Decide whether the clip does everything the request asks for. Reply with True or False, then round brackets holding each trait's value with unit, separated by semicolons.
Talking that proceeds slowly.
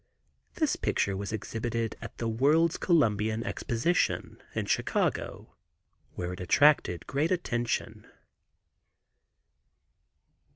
True (90 wpm)